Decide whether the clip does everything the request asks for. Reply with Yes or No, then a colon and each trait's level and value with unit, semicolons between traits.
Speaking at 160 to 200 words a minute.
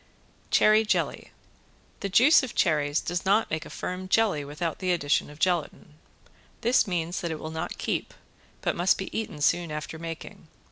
Yes: average, 175 wpm